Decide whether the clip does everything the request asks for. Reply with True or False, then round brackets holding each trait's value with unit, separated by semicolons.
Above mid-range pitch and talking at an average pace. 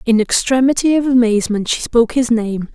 True (240 Hz; 175 wpm)